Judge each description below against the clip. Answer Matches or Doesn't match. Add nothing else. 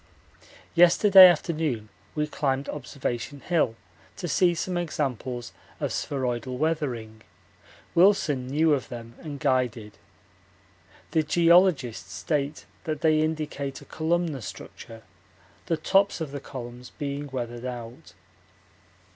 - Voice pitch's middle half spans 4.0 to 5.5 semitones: Matches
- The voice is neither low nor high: Matches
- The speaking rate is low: Matches